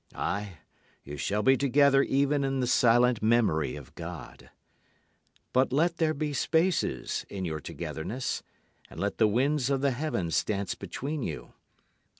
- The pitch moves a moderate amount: No, wide, 5.9 semitones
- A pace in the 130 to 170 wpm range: Yes, average, 150 wpm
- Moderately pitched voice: No, low, 125 Hz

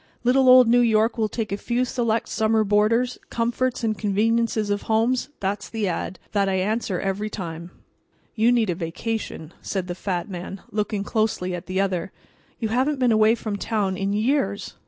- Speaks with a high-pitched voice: Yes, high, 215 Hz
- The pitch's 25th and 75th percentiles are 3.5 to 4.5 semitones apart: No, average, 3.1 semitones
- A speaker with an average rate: Yes, average, 175 wpm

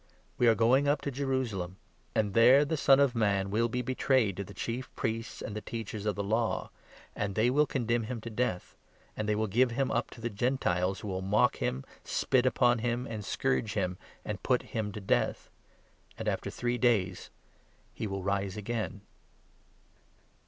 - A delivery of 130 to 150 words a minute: No, average, 195 wpm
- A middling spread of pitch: Yes, average, 3.6 semitones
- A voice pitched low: Yes, low, 115 Hz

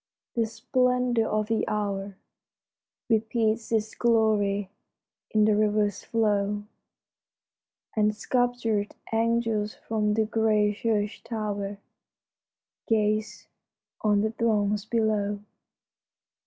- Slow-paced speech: Yes, slow, 90 wpm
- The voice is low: No, high, 215 Hz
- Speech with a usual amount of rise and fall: No, narrow, 1.4 semitones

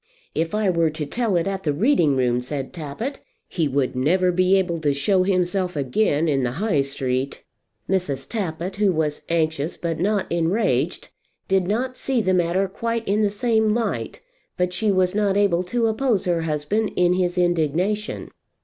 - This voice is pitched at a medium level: Yes, medium, 180 Hz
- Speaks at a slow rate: No, average, 175 wpm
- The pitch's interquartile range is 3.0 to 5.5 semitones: Yes, average, 4.7 semitones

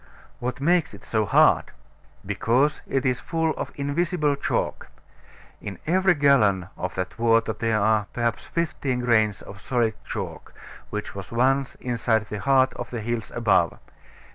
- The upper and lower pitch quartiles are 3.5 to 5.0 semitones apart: Yes, average, 4.5 semitones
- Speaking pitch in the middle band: No, low, 120 Hz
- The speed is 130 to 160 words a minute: Yes, average, 150 wpm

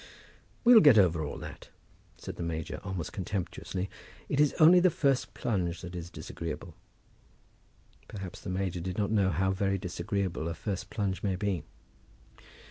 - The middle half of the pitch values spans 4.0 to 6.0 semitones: No, average, 3.0 semitones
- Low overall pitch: Yes, very low, 95 Hz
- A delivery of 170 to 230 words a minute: No, average, 155 wpm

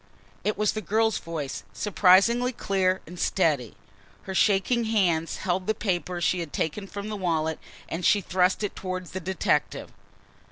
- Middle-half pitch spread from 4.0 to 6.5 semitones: No, average, 3.5 semitones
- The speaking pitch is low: No, medium, 185 Hz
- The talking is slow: No, average, 160 wpm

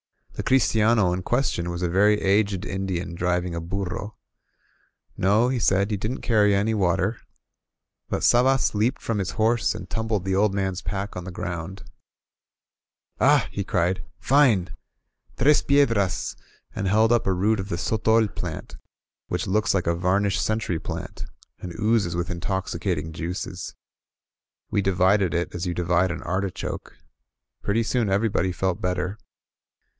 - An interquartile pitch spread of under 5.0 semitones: Yes, average, 3.3 semitones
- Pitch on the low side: Yes, very low, 95 Hz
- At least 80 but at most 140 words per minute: No, average, 150 wpm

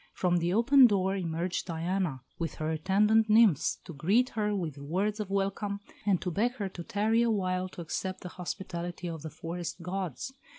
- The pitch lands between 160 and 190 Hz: Yes, medium, 185 Hz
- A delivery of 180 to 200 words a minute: Yes, average, 185 wpm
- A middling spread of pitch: Yes, average, 3.5 semitones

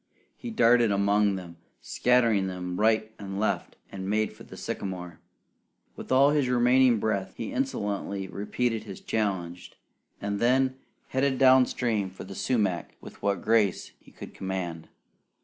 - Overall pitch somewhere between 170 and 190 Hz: No, low, 105 Hz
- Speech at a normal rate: Yes, average, 150 wpm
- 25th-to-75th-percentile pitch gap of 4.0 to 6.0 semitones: Yes, average, 4.4 semitones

